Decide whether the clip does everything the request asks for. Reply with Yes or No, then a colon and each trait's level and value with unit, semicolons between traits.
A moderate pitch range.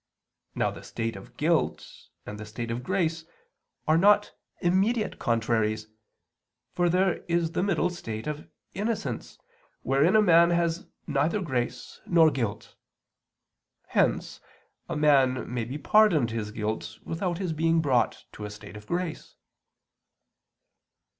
No: wide, 7.0 semitones